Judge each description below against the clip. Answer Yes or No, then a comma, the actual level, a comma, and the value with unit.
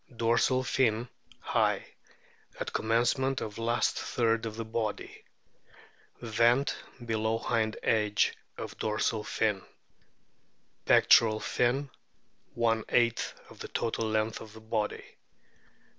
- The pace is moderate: No, slow, 110 wpm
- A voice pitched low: Yes, low, 115 Hz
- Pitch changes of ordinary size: No, narrow, 1.4 semitones